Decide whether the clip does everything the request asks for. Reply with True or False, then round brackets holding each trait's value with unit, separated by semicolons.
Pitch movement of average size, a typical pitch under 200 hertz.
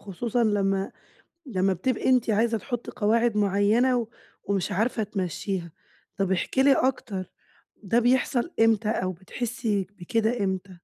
False (3.6 semitones; 210 Hz)